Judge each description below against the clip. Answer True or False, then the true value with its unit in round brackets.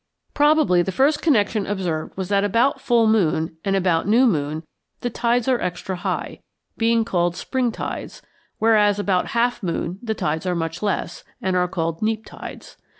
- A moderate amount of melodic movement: True (4.8 semitones)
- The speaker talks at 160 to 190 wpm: True (170 wpm)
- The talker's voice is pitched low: False (205 Hz)